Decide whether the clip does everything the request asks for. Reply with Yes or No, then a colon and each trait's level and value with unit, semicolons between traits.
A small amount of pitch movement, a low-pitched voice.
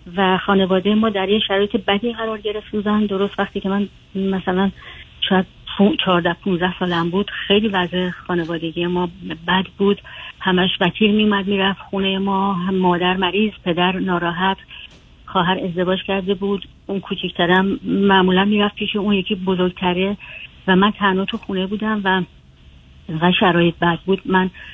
No: narrow, 1.7 semitones; high, 190 Hz